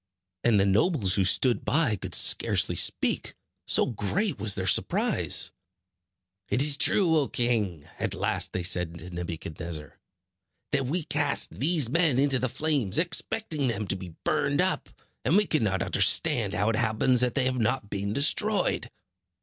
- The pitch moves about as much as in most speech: No, wide, 7.1 semitones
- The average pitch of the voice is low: Yes, low, 120 Hz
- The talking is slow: No, average, 160 wpm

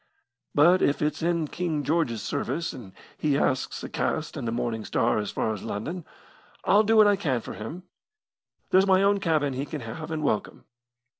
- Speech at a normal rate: Yes, average, 195 wpm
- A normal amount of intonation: No, wide, 6.3 semitones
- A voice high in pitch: No, medium, 150 Hz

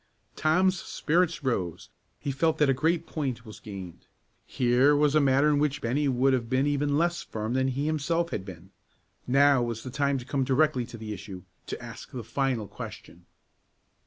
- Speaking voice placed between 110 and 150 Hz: Yes, low, 135 Hz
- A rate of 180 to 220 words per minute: Yes, average, 190 wpm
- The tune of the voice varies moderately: Yes, average, 4.1 semitones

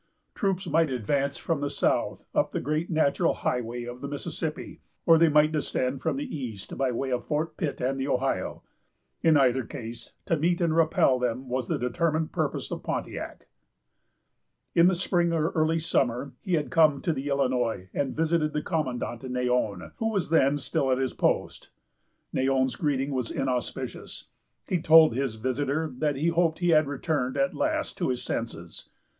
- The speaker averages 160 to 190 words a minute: Yes, average, 175 wpm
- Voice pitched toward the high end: No, medium, 140 Hz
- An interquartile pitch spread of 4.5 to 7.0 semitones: No, average, 4.1 semitones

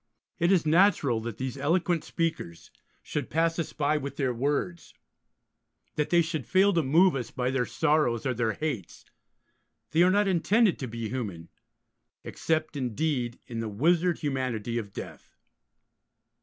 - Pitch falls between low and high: Yes, medium, 145 Hz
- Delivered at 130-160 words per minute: Yes, average, 155 wpm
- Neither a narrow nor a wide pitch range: No, wide, 5.7 semitones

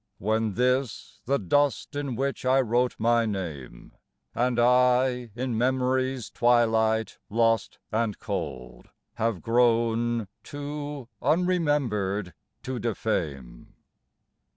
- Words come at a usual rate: No, slow, 100 wpm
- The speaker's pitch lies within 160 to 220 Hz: No, low, 120 Hz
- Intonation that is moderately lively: Yes, average, 3.1 semitones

